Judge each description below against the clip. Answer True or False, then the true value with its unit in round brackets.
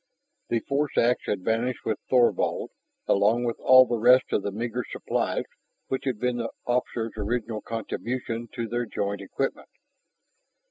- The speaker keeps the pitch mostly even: True (2.1 semitones)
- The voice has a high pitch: False (120 Hz)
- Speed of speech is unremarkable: True (150 wpm)